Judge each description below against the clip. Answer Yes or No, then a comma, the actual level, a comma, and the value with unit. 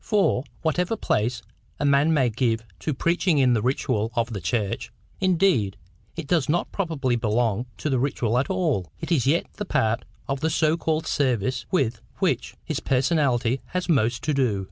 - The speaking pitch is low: Yes, low, 130 Hz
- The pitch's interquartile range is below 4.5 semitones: No, wide, 5.6 semitones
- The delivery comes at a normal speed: Yes, average, 170 wpm